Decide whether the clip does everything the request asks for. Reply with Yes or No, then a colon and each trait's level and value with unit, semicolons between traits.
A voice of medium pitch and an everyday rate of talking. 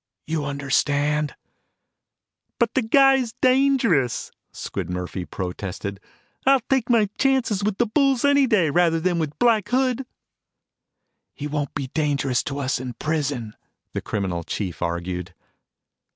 No: medium, 155 Hz; slow, 130 wpm